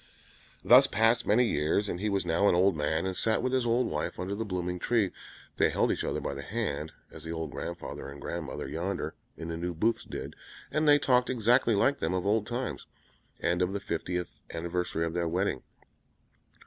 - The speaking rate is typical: No, fast, 210 wpm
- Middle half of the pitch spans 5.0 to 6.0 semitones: Yes, average, 5.3 semitones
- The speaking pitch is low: Yes, very low, 90 Hz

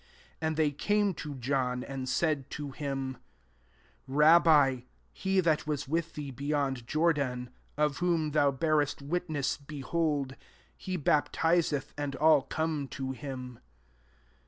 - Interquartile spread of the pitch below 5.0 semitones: Yes, average, 2.9 semitones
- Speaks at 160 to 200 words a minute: No, slow, 135 wpm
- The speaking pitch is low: No, medium, 145 Hz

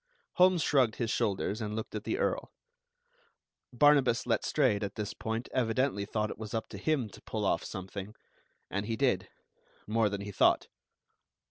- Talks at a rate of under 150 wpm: No, average, 165 wpm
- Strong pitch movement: No, average, 3.8 semitones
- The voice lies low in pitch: Yes, low, 110 Hz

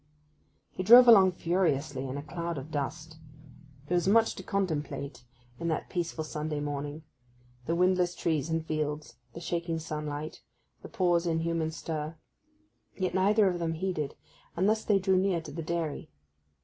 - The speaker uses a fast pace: No, average, 160 wpm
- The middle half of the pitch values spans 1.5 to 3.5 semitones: Yes, average, 3.2 semitones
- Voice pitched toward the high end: No, medium, 165 Hz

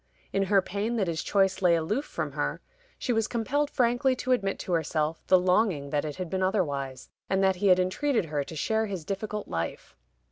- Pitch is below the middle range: No, high, 190 Hz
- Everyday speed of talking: No, fast, 210 wpm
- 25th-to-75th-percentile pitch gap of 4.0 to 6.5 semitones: Yes, average, 5.1 semitones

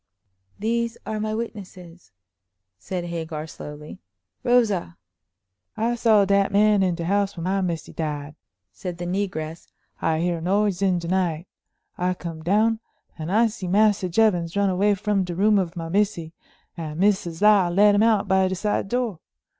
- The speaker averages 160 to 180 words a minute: Yes, average, 165 wpm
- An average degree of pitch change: Yes, average, 3.6 semitones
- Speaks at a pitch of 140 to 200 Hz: Yes, high, 190 Hz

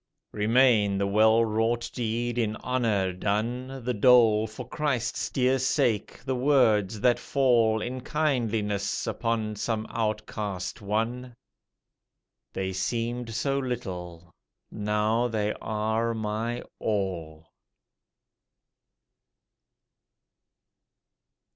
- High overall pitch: No, low, 110 Hz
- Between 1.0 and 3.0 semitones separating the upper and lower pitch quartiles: Yes, narrow, 2.6 semitones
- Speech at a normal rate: No, slow, 90 wpm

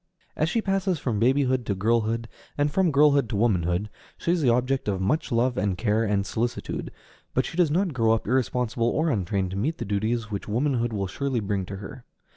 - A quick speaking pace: Yes, fast, 210 wpm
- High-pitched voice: No, low, 120 Hz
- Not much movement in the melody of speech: No, average, 5.3 semitones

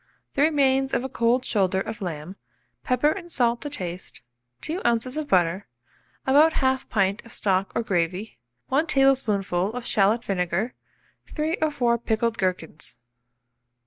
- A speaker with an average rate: Yes, average, 145 wpm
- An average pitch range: No, wide, 5.9 semitones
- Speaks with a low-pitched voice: No, high, 235 Hz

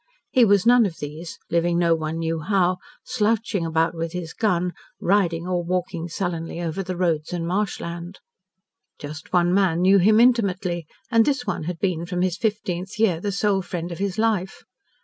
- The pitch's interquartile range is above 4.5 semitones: No, average, 3.0 semitones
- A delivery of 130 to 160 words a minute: No, average, 180 wpm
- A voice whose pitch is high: No, medium, 180 Hz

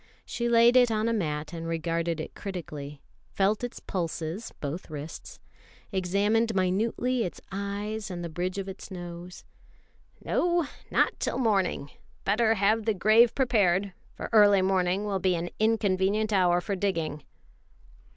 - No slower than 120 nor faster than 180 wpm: Yes, average, 145 wpm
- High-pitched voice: Yes, high, 195 Hz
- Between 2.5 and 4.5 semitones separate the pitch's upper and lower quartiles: Yes, average, 3.8 semitones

